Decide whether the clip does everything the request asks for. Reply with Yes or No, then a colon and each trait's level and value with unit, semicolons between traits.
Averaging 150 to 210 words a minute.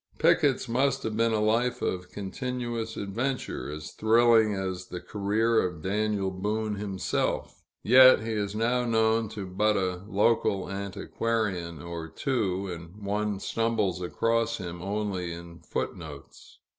No: average, 140 wpm